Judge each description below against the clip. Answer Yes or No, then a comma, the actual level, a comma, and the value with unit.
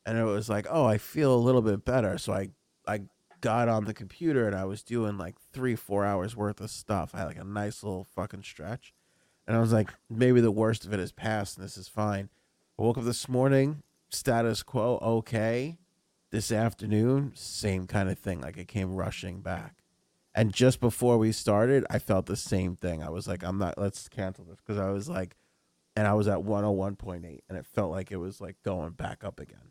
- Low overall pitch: Yes, low, 105 Hz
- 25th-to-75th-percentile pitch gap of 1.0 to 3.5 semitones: Yes, average, 3.2 semitones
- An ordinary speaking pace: No, fast, 220 wpm